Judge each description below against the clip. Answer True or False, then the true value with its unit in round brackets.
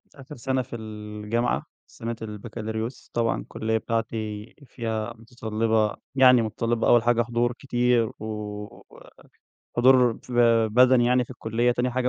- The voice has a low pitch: True (115 Hz)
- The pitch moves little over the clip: True (1.9 semitones)